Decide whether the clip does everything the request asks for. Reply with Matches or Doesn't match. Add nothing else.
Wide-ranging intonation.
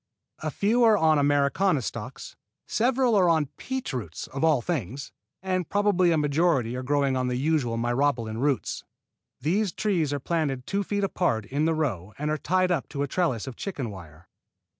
Matches